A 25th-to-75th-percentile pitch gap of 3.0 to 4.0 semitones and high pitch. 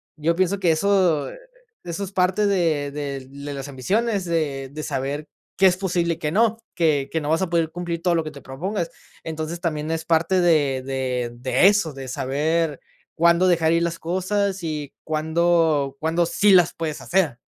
No: average, 3.5 semitones; medium, 165 Hz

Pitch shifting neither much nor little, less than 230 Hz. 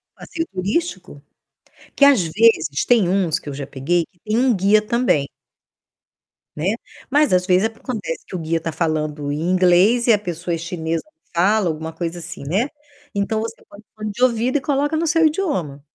No: wide, 6.3 semitones; high, 190 Hz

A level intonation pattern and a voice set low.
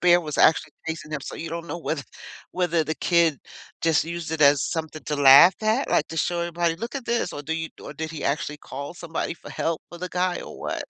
No: narrow, 2.0 semitones; medium, 165 Hz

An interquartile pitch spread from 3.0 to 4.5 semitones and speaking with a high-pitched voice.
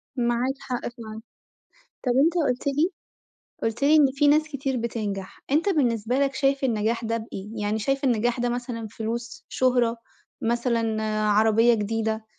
Yes: average, 3.3 semitones; high, 235 Hz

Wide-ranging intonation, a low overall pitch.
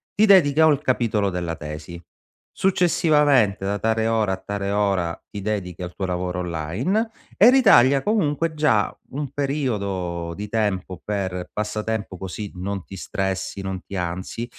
Yes: wide, 6.9 semitones; low, 100 Hz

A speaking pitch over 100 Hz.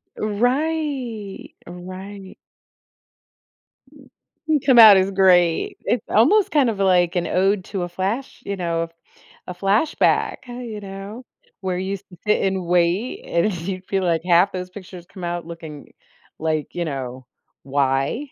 Yes: high, 190 Hz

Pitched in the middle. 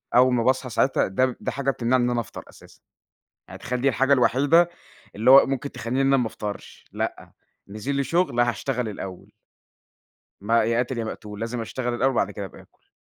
No: low, 125 Hz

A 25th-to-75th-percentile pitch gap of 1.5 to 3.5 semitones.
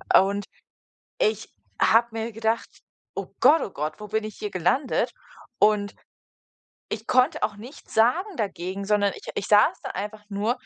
Yes: narrow, 2.6 semitones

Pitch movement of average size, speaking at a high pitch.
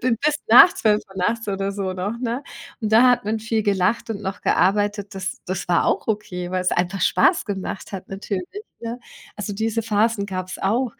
Yes: average, 3.0 semitones; high, 205 Hz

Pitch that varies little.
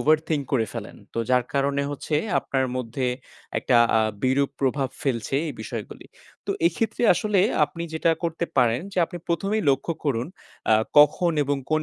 No: average, 4.0 semitones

